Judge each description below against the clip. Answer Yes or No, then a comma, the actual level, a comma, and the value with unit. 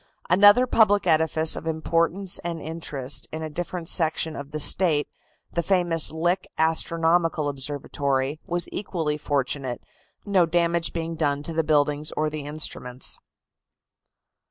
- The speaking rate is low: Yes, slow, 130 wpm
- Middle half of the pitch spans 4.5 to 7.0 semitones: No, narrow, 2.6 semitones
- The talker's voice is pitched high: No, medium, 160 Hz